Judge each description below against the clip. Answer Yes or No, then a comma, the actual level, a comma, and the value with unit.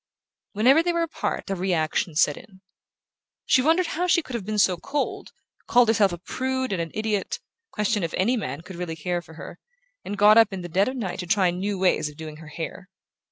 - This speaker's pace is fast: Yes, fast, 220 wpm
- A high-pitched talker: Yes, high, 195 Hz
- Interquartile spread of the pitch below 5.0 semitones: No, wide, 5.4 semitones